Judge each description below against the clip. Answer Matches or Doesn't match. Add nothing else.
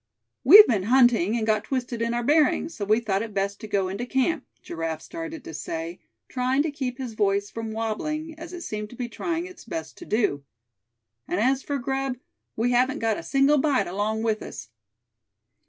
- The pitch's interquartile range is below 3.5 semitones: Doesn't match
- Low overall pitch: Doesn't match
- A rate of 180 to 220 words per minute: Matches